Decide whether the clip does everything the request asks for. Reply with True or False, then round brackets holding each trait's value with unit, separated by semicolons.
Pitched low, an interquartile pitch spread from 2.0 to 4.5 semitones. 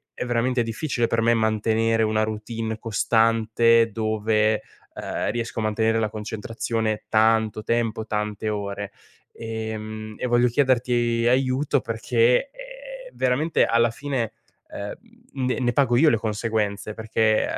False (115 Hz; 1.5 semitones)